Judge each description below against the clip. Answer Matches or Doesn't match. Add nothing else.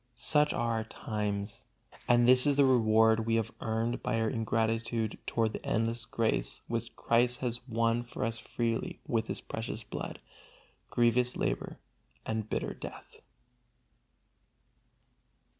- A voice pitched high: Doesn't match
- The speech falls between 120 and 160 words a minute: Matches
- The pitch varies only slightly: Matches